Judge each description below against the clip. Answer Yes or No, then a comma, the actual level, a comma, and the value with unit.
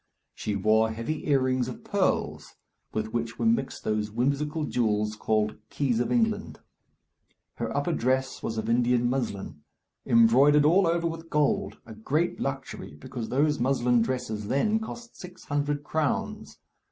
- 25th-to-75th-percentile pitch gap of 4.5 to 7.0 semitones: Yes, average, 5.0 semitones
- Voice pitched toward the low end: Yes, low, 130 Hz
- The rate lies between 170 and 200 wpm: No, average, 145 wpm